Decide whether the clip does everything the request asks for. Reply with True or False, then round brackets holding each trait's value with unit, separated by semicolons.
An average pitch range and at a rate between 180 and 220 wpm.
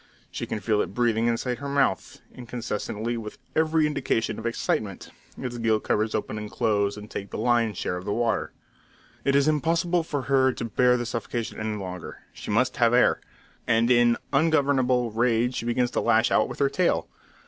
True (3.0 semitones; 190 wpm)